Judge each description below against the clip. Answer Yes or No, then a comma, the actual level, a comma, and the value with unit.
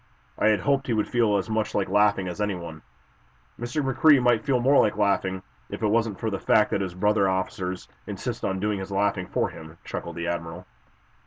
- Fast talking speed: Yes, fast, 210 wpm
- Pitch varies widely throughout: No, average, 3.2 semitones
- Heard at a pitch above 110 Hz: No, low, 105 Hz